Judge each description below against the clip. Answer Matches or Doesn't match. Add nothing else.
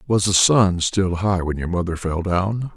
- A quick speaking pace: Matches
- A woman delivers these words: Doesn't match